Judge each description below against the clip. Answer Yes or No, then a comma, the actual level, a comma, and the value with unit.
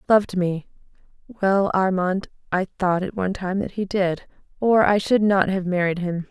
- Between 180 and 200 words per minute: No, average, 170 wpm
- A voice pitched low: No, high, 190 Hz